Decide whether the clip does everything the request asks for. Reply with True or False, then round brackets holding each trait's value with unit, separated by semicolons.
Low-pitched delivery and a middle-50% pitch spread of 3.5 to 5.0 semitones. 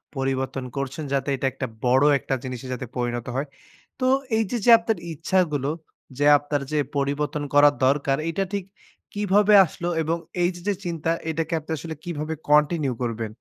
False (145 Hz; 3.9 semitones)